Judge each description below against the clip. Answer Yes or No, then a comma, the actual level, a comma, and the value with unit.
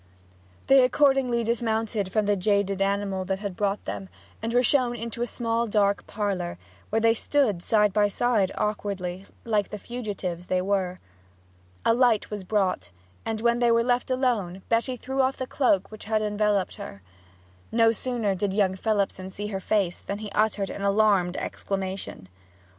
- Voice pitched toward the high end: Yes, high, 210 Hz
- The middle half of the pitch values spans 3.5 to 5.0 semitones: No, average, 3.1 semitones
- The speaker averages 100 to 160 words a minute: No, average, 170 wpm